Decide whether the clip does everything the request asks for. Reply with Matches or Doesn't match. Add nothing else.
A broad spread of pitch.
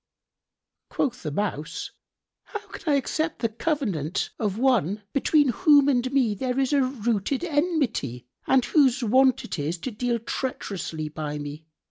Matches